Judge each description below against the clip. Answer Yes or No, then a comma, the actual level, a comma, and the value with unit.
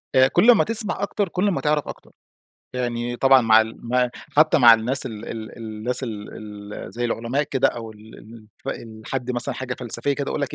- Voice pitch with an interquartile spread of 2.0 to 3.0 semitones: No, average, 3.7 semitones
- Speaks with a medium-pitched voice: No, low, 125 Hz